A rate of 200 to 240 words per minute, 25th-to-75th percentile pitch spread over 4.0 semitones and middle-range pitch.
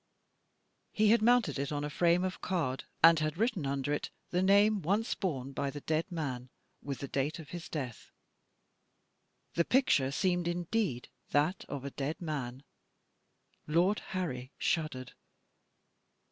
No: average, 145 wpm; average, 4.9 semitones; medium, 155 Hz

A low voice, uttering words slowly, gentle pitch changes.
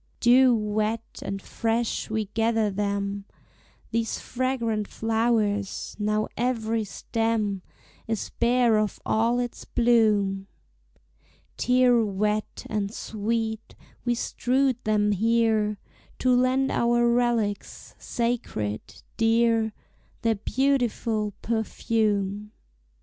No: high, 225 Hz; slow, 95 wpm; narrow, 2.1 semitones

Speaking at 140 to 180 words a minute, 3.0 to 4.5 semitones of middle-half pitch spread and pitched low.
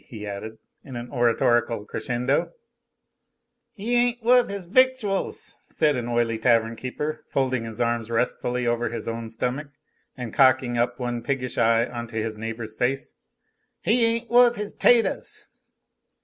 No: average, 150 wpm; average, 5.1 semitones; low, 120 Hz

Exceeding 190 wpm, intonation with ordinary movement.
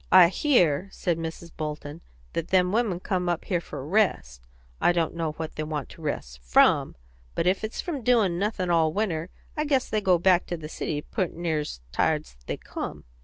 Yes: average, 200 wpm; average, 3.6 semitones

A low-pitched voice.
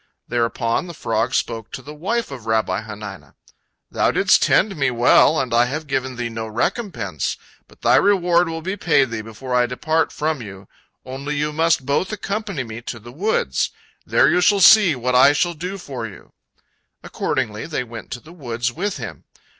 Yes: low, 130 Hz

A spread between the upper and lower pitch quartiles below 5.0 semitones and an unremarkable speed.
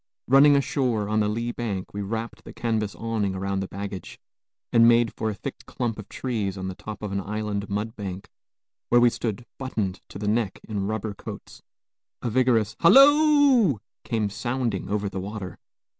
Yes: average, 2.9 semitones; average, 175 wpm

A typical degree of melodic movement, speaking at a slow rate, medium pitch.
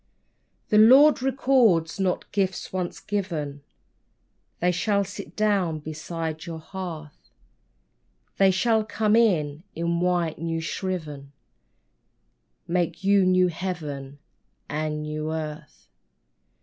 Yes: average, 4.1 semitones; slow, 110 wpm; medium, 175 Hz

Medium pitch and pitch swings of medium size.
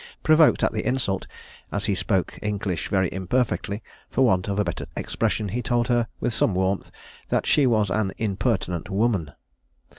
No: low, 105 Hz; average, 3.9 semitones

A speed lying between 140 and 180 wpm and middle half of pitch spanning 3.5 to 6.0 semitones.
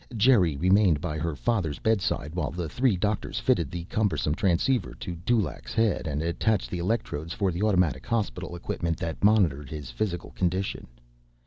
Yes: average, 160 wpm; average, 4.7 semitones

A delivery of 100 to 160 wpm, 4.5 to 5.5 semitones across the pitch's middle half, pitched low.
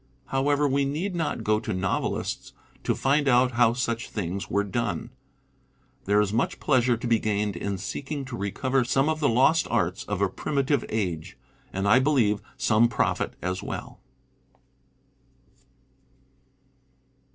Yes: average, 150 wpm; average, 5.1 semitones; low, 120 Hz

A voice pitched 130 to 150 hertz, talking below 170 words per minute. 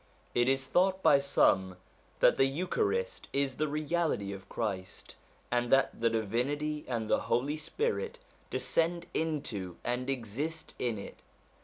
Yes: low, 135 Hz; average, 140 wpm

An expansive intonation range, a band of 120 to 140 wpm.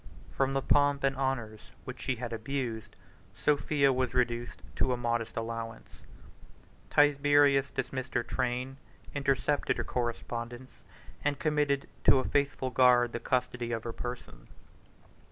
No: narrow, 2.6 semitones; slow, 135 wpm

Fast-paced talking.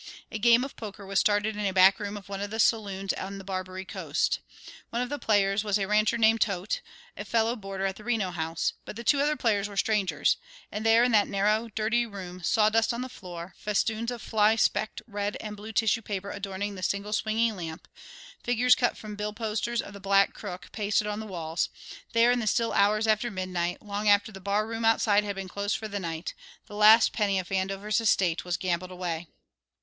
Yes: fast, 215 wpm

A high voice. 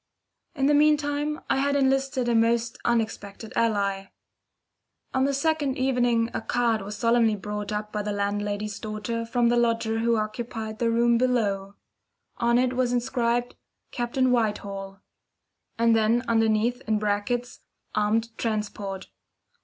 Yes: high, 230 Hz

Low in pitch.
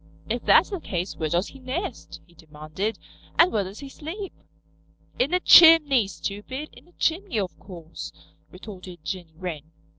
No: high, 200 Hz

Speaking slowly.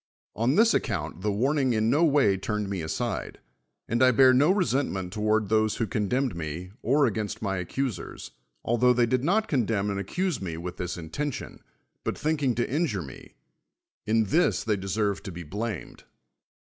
No: average, 175 wpm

